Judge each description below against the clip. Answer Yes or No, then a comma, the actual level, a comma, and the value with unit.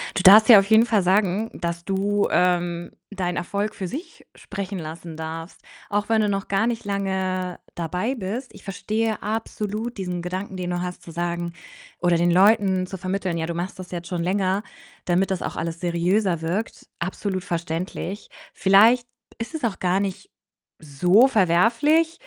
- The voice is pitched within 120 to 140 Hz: No, high, 190 Hz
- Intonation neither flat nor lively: Yes, average, 3.1 semitones